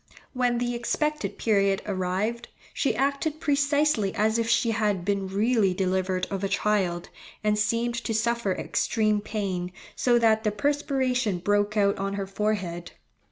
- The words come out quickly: No, average, 150 wpm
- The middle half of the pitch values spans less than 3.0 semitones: No, average, 3.4 semitones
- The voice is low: No, high, 215 Hz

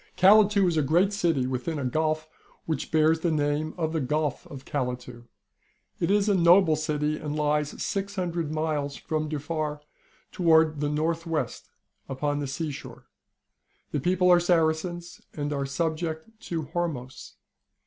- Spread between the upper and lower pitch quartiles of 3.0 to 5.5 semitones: No, narrow, 2.6 semitones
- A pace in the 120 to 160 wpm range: Yes, average, 150 wpm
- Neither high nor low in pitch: Yes, medium, 155 Hz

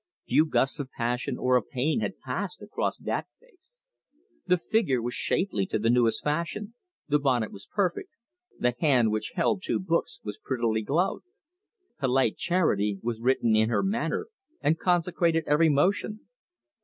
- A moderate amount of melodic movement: No, wide, 7.1 semitones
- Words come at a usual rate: Yes, average, 155 wpm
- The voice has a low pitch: No, medium, 145 Hz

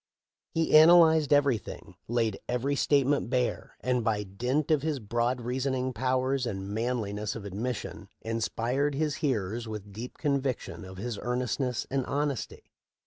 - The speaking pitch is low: Yes, low, 125 Hz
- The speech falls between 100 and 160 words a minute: Yes, average, 150 wpm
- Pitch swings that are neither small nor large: Yes, average, 3.7 semitones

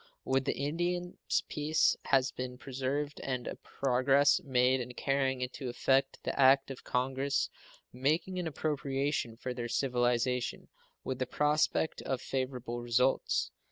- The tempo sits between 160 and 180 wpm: No, slow, 135 wpm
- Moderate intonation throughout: No, narrow, 2.0 semitones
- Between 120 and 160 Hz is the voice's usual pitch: Yes, low, 135 Hz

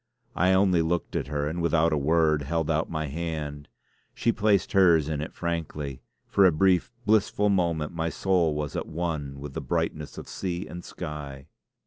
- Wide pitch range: No, average, 2.8 semitones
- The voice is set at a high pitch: No, very low, 80 Hz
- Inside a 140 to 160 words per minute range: No, average, 180 wpm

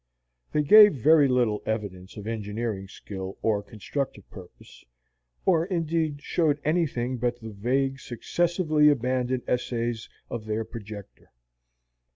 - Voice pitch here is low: Yes, low, 120 Hz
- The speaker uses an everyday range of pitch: No, wide, 5.7 semitones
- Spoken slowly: Yes, slow, 120 wpm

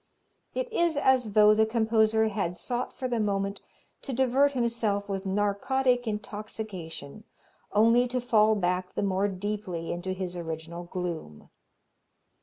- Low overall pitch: No, high, 210 Hz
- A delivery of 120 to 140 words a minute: Yes, slow, 135 wpm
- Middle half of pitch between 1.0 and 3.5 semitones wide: No, average, 4.1 semitones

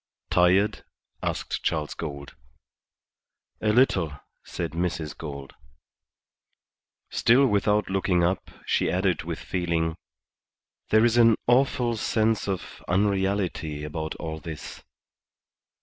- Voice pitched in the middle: No, very low, 90 Hz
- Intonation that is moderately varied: Yes, average, 5.0 semitones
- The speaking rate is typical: No, slow, 100 wpm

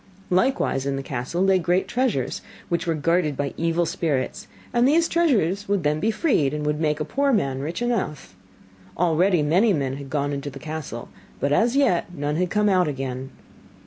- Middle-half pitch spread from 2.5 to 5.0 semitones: No, wide, 5.6 semitones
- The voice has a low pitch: No, medium, 165 Hz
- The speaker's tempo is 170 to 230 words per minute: Yes, average, 190 wpm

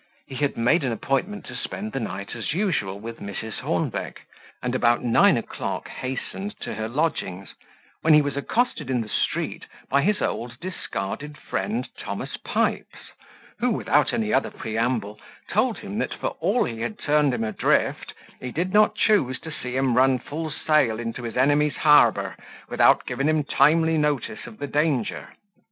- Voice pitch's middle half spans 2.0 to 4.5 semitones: No, wide, 5.4 semitones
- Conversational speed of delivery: Yes, average, 170 wpm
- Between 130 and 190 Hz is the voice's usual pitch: Yes, medium, 140 Hz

